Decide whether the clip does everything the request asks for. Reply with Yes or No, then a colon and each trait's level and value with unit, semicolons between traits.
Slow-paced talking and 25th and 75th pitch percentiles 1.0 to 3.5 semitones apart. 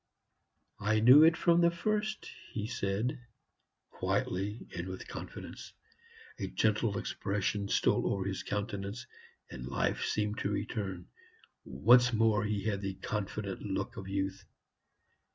Yes: slow, 130 wpm; average, 3.2 semitones